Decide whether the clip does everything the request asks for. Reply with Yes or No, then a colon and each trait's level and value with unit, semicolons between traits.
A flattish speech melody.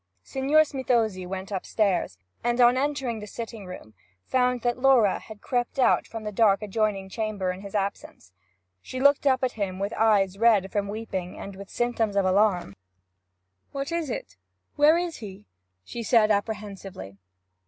No: average, 4.0 semitones